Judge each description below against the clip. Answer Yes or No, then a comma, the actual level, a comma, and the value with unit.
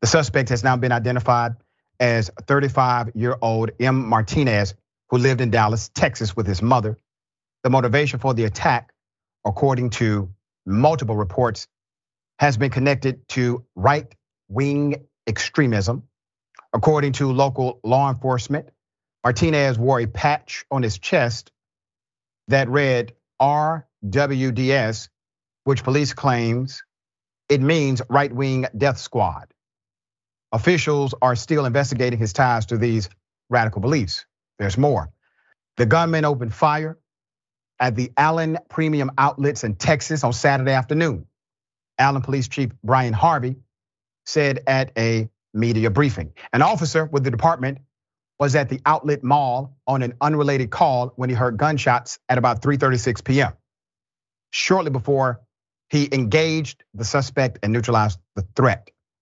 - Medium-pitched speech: No, low, 130 Hz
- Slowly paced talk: Yes, slow, 130 wpm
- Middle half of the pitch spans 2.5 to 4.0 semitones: Yes, average, 3.5 semitones